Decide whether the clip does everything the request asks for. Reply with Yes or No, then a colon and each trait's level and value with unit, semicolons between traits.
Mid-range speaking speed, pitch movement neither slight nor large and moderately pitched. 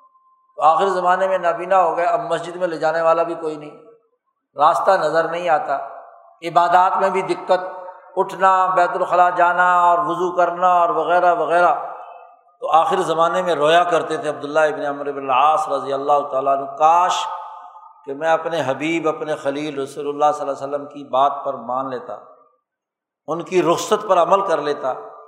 Yes: average, 175 wpm; average, 3.2 semitones; medium, 170 Hz